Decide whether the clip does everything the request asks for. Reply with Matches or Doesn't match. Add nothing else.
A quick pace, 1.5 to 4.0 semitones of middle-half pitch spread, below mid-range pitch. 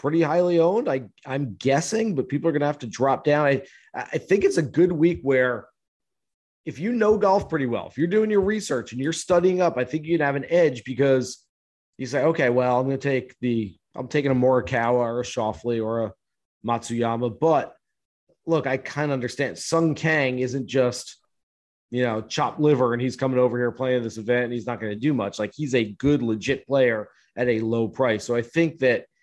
Doesn't match